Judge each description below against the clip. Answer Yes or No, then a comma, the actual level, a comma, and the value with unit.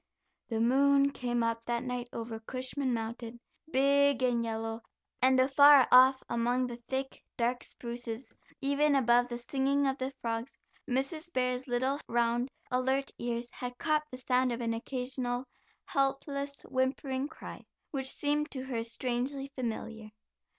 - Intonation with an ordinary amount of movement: No, narrow, 2.3 semitones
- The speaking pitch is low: No, very high, 255 Hz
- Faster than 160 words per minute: No, average, 145 wpm